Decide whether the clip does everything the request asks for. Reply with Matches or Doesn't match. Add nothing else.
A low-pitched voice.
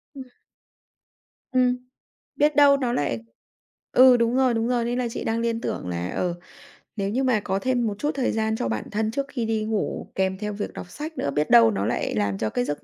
Doesn't match